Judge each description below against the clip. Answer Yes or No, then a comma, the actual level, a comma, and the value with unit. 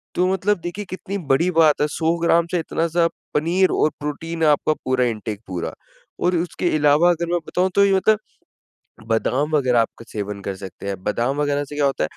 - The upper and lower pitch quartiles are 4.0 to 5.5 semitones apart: Yes, average, 5.1 semitones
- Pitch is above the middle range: No, medium, 155 Hz